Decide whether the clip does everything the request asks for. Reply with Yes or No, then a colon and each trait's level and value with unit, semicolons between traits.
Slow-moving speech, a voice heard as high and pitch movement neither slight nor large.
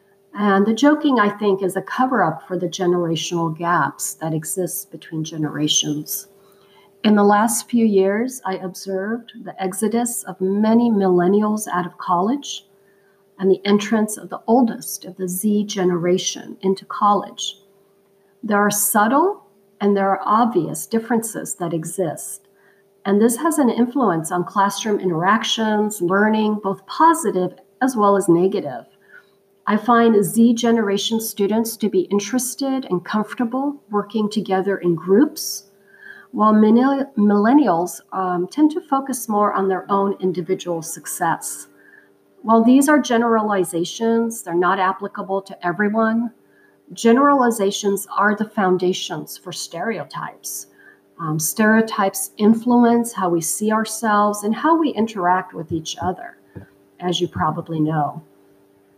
Yes: slow, 130 wpm; high, 200 Hz; average, 3.5 semitones